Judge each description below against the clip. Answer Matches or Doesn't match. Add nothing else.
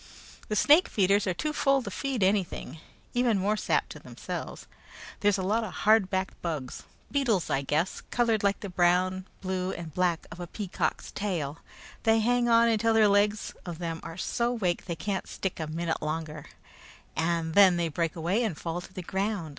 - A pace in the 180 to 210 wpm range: Matches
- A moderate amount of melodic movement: Matches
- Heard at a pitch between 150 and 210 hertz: Matches